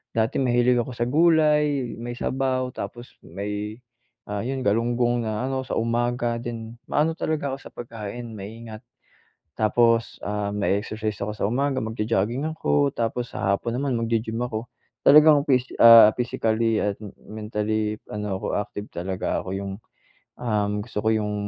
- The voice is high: No, low, 115 Hz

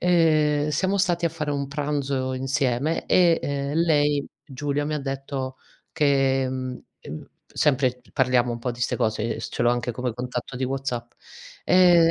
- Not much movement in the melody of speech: No, average, 3.0 semitones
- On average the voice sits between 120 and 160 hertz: Yes, low, 135 Hz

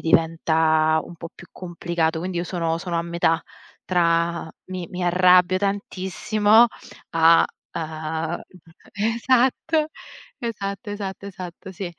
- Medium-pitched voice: Yes, medium, 175 Hz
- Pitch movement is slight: No, average, 3.1 semitones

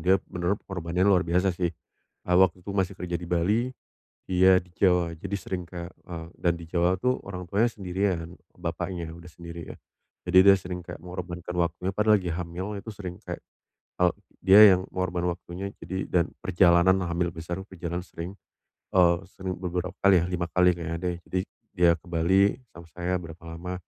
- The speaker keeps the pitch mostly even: Yes, narrow, 1.6 semitones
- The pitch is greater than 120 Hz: No, very low, 90 Hz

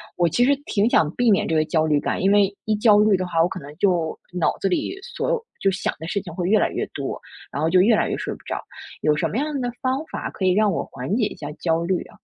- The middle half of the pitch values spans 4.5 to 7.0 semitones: Yes, average, 4.8 semitones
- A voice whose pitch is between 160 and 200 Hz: Yes, high, 190 Hz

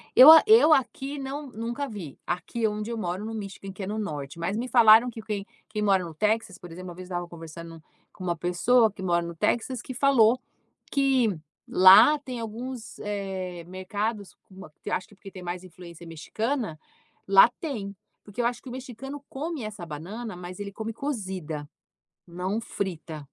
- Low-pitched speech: No, high, 205 Hz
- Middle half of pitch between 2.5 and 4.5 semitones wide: No, average, 5.0 semitones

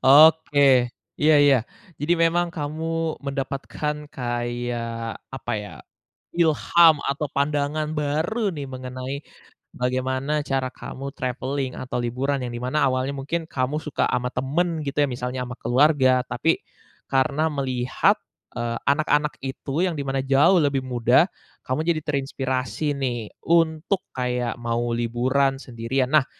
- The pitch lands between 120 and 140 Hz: Yes, low, 135 Hz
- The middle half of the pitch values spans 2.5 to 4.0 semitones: Yes, average, 3.1 semitones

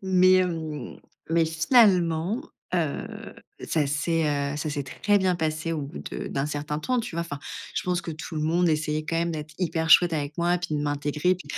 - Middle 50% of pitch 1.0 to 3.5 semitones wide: Yes, average, 2.8 semitones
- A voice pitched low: No, medium, 160 Hz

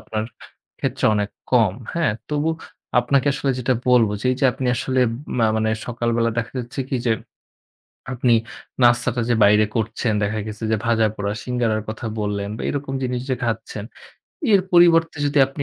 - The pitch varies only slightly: No, average, 3.0 semitones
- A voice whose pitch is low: Yes, low, 120 Hz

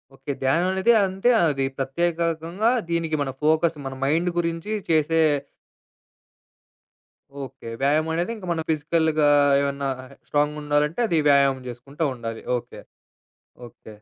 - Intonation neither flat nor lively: Yes, average, 3.2 semitones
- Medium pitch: Yes, medium, 155 Hz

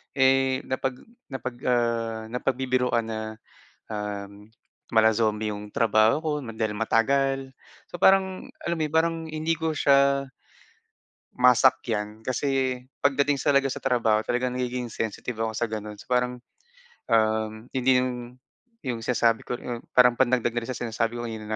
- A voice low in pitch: Yes, low, 125 Hz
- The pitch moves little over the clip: No, average, 3.0 semitones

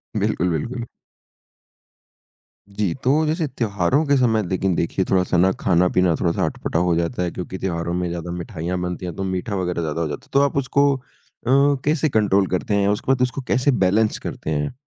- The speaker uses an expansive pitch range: Yes, wide, 6.3 semitones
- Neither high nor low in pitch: No, very low, 95 Hz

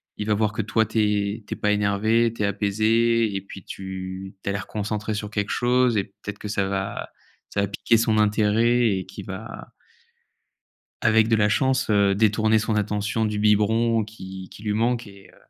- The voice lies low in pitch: Yes, low, 105 Hz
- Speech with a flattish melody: Yes, narrow, 1.8 semitones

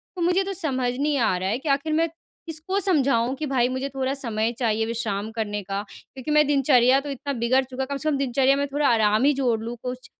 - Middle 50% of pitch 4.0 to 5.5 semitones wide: No, average, 3.5 semitones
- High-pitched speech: Yes, very high, 265 Hz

